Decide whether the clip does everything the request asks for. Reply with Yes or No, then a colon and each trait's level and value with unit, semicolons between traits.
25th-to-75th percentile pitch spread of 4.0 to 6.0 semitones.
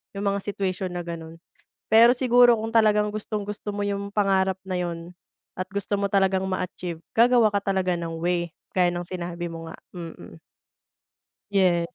No: average, 2.7 semitones